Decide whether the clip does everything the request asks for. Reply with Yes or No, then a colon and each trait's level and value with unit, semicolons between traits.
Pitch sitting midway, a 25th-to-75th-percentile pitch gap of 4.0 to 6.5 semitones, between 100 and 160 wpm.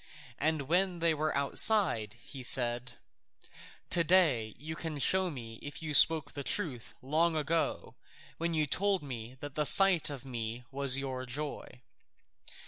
Yes: medium, 145 Hz; average, 4.4 semitones; average, 145 wpm